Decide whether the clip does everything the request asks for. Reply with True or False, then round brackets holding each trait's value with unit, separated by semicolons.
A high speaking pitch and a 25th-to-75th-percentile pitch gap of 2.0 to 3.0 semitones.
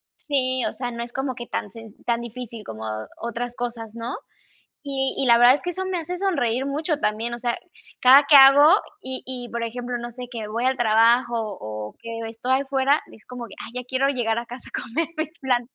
True (245 Hz; 2.5 semitones)